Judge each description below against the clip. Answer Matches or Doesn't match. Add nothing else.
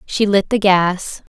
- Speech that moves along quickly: Doesn't match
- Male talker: Doesn't match